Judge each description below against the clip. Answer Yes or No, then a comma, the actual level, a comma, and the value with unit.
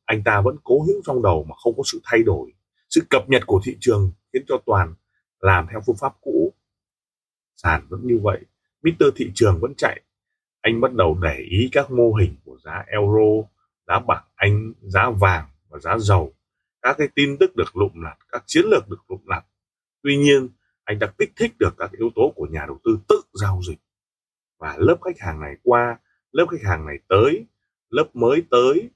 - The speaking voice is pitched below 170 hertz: Yes, medium, 140 Hz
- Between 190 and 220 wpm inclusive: Yes, average, 205 wpm